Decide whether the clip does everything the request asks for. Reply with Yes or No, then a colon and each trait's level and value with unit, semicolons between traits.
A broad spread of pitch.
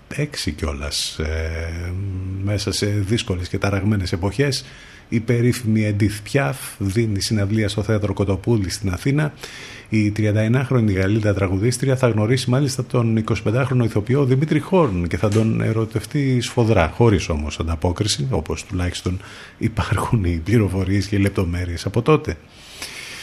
No: average, 4.2 semitones